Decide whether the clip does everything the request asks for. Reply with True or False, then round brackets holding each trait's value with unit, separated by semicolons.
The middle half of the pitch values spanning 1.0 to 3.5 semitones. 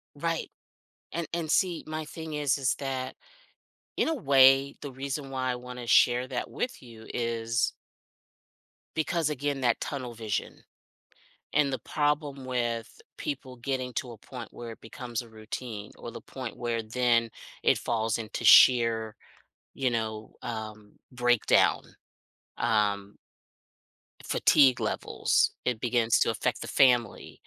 True (3.1 semitones)